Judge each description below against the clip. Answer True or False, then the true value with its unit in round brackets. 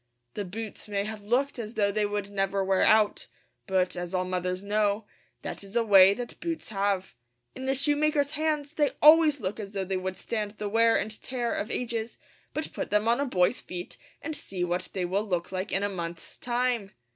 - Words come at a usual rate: False (210 wpm)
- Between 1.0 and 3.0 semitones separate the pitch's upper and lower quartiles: False (4.1 semitones)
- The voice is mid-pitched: False (210 Hz)